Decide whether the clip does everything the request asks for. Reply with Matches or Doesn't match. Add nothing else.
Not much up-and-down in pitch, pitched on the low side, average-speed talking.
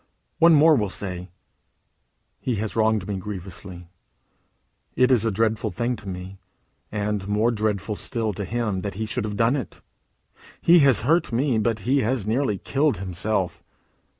Doesn't match